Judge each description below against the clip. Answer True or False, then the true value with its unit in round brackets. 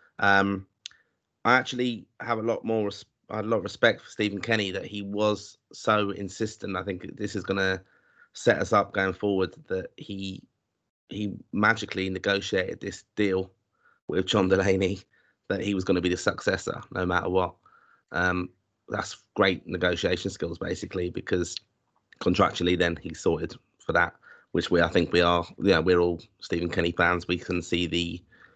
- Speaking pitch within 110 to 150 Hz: False (95 Hz)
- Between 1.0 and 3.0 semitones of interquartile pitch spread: True (2.4 semitones)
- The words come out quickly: False (170 wpm)